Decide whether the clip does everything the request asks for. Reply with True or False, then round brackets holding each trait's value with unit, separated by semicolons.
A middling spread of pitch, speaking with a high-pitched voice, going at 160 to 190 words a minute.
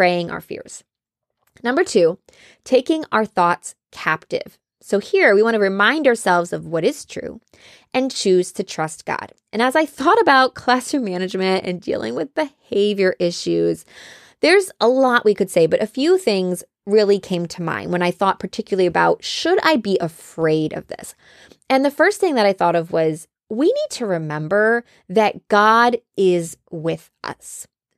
False (6.5 semitones; 205 Hz; 170 wpm)